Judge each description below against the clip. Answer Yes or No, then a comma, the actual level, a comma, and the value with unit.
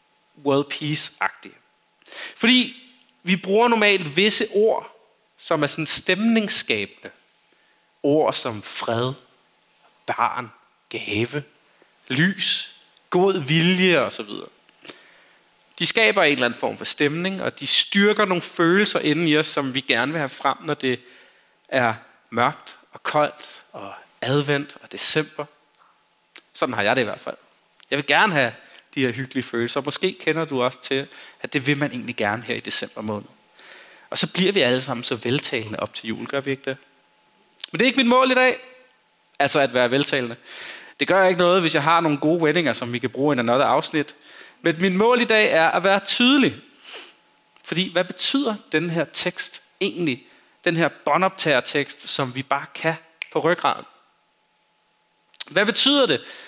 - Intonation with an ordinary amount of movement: No, wide, 5.9 semitones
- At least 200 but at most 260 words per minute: No, average, 170 wpm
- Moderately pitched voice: Yes, medium, 155 Hz